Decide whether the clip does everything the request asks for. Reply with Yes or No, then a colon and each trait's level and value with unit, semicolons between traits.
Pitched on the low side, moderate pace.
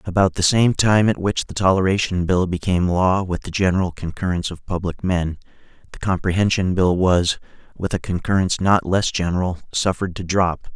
Yes: very low, 90 Hz; average, 175 wpm